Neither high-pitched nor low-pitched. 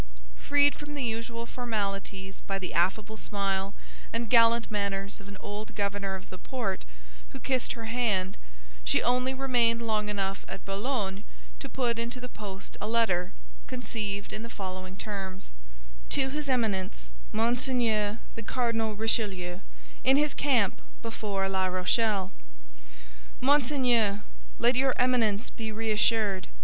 No: high, 220 Hz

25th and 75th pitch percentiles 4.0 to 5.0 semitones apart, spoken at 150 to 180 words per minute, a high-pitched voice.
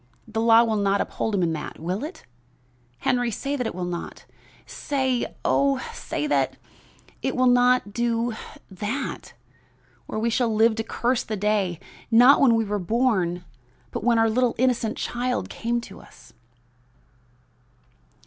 No: average, 3.3 semitones; average, 155 wpm; high, 230 Hz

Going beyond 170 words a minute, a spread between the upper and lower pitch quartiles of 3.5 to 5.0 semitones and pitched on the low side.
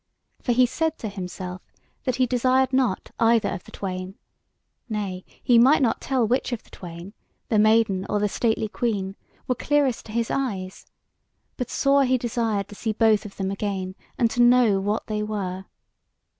No: average, 180 wpm; average, 4.1 semitones; high, 220 Hz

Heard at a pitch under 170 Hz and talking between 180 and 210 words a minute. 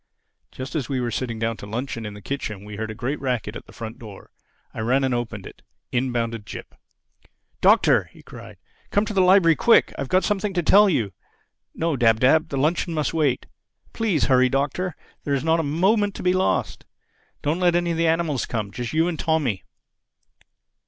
Yes: medium, 140 Hz; average, 195 wpm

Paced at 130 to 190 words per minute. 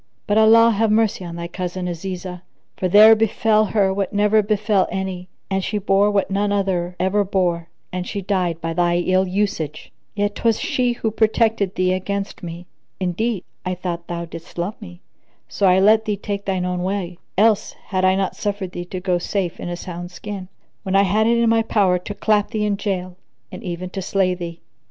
No: average, 200 wpm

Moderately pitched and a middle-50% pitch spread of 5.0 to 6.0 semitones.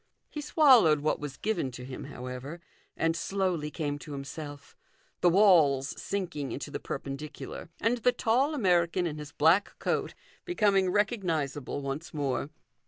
Yes: medium, 165 Hz; wide, 5.6 semitones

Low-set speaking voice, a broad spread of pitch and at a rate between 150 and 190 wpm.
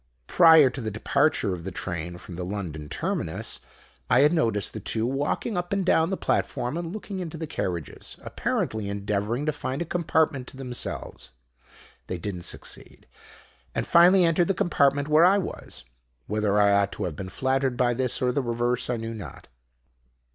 Yes: low, 125 Hz; wide, 7.8 semitones; average, 185 wpm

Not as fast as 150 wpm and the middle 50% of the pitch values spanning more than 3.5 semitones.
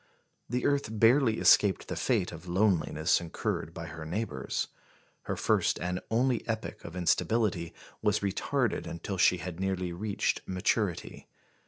Yes: average, 140 wpm; average, 4.2 semitones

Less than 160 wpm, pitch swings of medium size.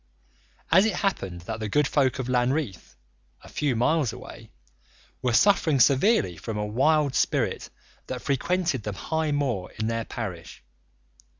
No: average, 145 wpm; wide, 5.9 semitones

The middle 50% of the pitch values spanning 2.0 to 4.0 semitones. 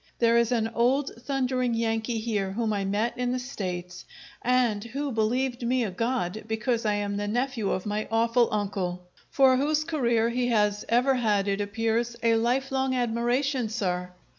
Yes: average, 3.3 semitones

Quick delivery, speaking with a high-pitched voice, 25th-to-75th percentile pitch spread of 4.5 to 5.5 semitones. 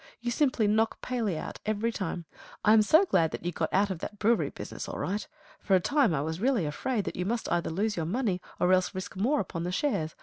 Yes: fast, 245 wpm; high, 205 Hz; average, 4.8 semitones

